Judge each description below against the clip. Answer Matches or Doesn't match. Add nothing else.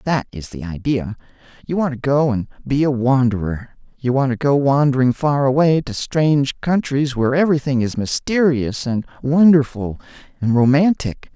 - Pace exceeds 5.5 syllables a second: Doesn't match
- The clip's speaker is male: Matches